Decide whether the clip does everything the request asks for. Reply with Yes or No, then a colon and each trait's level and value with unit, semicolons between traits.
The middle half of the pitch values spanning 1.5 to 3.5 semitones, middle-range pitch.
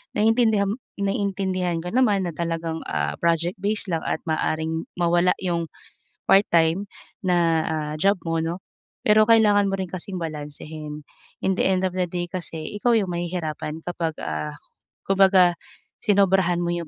Yes: average, 3.0 semitones; medium, 175 Hz